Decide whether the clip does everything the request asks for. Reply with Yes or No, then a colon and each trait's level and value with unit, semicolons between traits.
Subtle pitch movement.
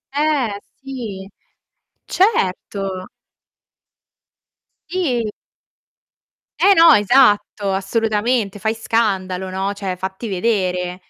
No: average, 4.3 semitones